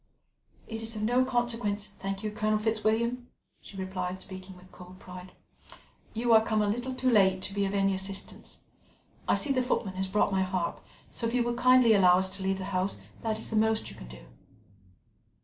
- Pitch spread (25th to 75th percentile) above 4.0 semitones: No, average, 3.3 semitones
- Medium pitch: No, high, 205 Hz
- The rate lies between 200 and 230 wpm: Yes, fast, 205 wpm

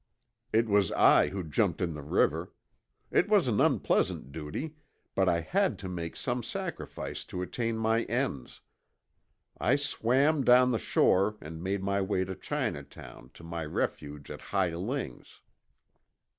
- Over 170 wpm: No, average, 150 wpm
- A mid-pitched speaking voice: No, low, 100 Hz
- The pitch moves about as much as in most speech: No, wide, 6.5 semitones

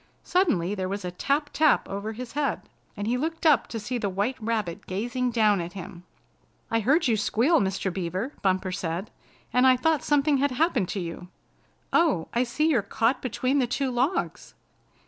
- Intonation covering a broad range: Yes, wide, 6.1 semitones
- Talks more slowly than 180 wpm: No, average, 185 wpm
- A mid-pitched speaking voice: No, high, 235 Hz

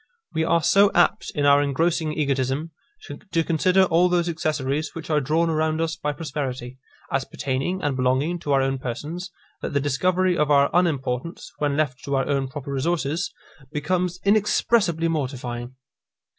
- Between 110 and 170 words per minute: Yes, average, 160 wpm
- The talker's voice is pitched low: No, medium, 150 Hz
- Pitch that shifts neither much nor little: Yes, average, 3.8 semitones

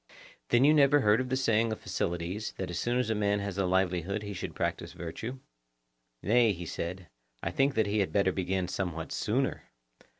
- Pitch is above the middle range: No, low, 100 Hz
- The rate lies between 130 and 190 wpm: No, average, 200 wpm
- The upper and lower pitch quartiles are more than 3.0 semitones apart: Yes, average, 4.1 semitones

